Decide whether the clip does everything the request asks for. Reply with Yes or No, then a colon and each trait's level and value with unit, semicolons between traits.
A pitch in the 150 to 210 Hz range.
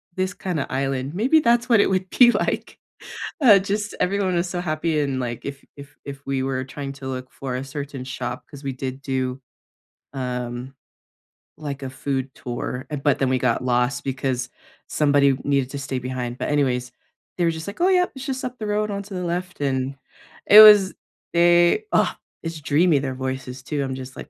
No: medium, 140 Hz